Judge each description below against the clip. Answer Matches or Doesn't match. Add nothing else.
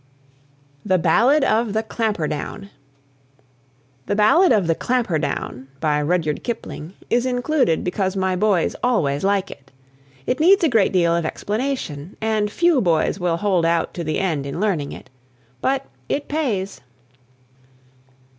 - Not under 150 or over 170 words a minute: Doesn't match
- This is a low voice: Doesn't match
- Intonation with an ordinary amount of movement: Doesn't match